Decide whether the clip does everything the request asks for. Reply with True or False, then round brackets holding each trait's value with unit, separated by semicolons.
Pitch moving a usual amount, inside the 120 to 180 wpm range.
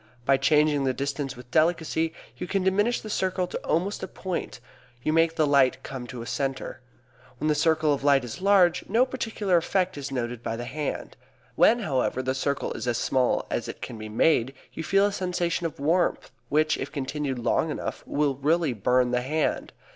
False (5.0 semitones; 200 wpm)